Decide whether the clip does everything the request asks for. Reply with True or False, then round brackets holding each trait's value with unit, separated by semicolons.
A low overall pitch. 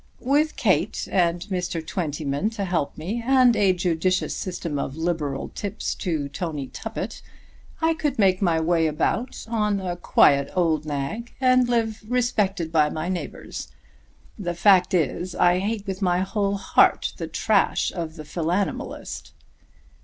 False (180 Hz)